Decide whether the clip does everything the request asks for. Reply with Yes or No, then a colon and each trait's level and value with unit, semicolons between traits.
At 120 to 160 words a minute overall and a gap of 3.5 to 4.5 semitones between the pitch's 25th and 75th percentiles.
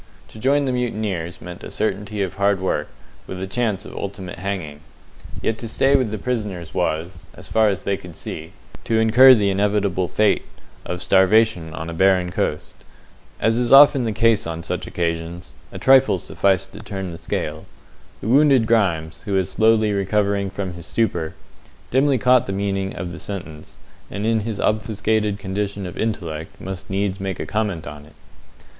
No: average, 175 wpm; average, 3.8 semitones